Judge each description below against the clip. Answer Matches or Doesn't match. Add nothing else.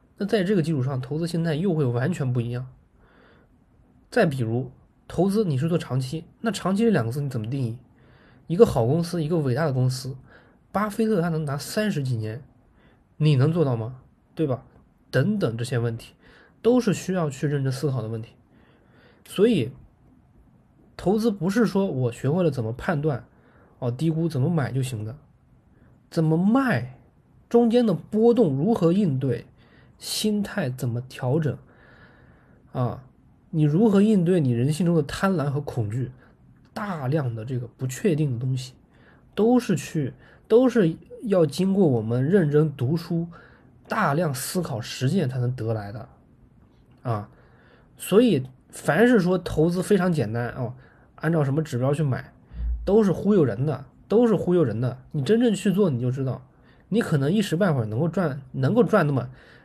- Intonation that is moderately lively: Doesn't match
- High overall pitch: Doesn't match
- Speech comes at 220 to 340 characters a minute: Matches